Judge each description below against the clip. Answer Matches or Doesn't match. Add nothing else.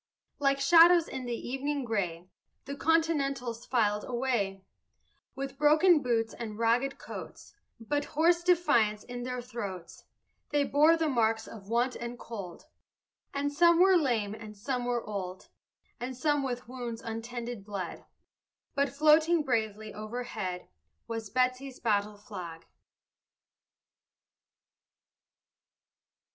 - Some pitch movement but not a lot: Matches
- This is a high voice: Matches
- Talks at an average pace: Doesn't match